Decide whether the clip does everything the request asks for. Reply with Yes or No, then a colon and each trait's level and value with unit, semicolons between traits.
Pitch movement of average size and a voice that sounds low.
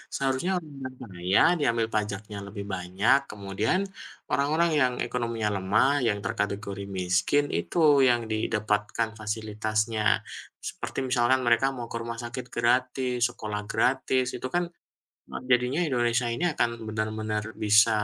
Yes: average, 3.2 semitones; low, 115 Hz